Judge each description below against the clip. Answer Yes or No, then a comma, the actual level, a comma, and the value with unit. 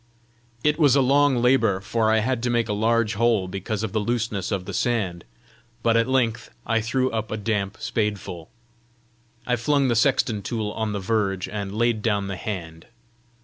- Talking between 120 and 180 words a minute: No, average, 190 wpm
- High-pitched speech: No, low, 110 Hz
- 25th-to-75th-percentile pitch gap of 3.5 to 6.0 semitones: No, average, 2.8 semitones